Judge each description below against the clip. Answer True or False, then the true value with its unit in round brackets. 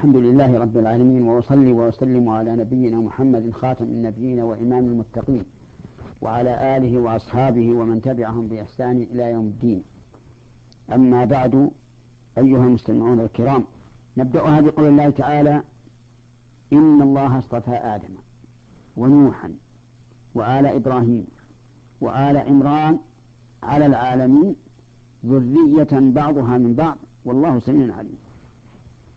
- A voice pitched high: False (125 Hz)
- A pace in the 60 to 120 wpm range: True (100 wpm)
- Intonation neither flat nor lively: False (2.2 semitones)